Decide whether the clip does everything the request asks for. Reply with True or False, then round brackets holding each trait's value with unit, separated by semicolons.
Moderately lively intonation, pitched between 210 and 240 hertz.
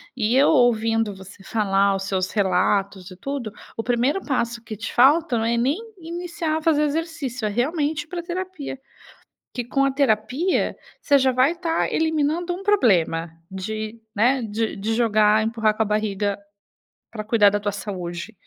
False (5.9 semitones; 230 Hz)